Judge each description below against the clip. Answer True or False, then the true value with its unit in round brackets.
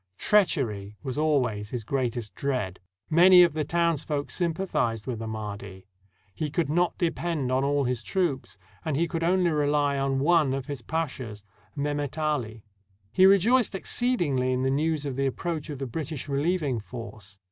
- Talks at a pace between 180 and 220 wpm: False (170 wpm)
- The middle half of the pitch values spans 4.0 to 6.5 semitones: True (4.9 semitones)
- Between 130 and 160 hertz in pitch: True (140 Hz)